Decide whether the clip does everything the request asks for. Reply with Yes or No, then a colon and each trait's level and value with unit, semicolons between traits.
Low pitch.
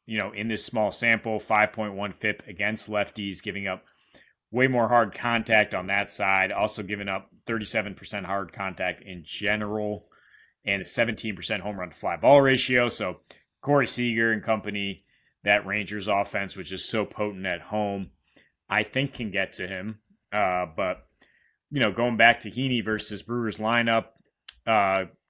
Yes: low, 105 Hz